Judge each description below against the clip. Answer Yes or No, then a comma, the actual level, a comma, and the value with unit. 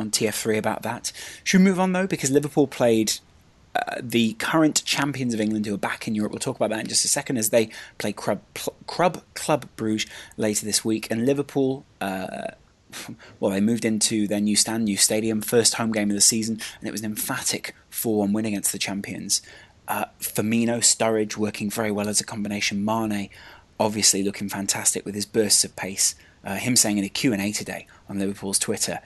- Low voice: Yes, low, 110 Hz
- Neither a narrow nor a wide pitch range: No, narrow, 2.1 semitones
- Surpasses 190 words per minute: Yes, average, 200 wpm